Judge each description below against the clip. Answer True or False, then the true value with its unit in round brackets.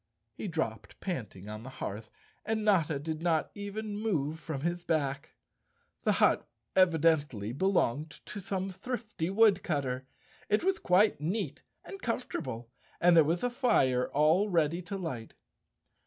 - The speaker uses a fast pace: False (145 wpm)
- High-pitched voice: False (165 Hz)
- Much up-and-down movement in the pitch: True (6.3 semitones)